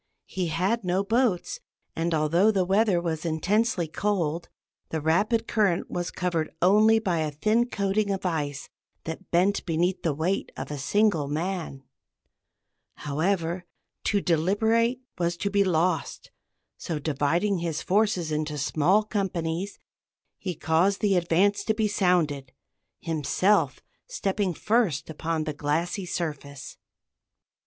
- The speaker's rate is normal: No, slow, 130 wpm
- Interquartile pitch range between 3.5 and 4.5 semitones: Yes, average, 4.1 semitones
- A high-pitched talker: No, medium, 175 Hz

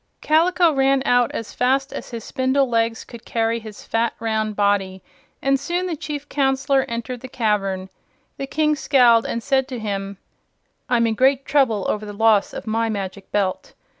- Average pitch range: Yes, average, 4.0 semitones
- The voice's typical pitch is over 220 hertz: Yes, high, 235 Hz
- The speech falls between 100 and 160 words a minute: No, average, 175 wpm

